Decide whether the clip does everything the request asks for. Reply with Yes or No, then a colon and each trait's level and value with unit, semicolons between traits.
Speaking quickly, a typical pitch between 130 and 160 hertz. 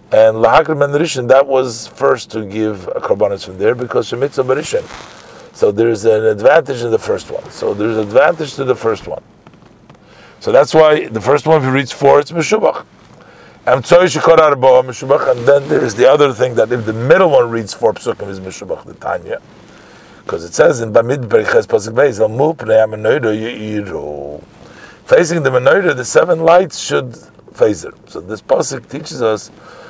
No: average, 185 wpm; medium, 140 Hz